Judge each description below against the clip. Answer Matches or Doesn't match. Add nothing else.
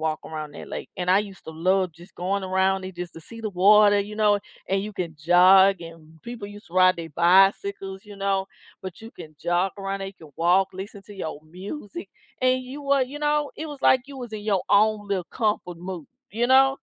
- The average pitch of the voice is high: Matches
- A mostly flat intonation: Doesn't match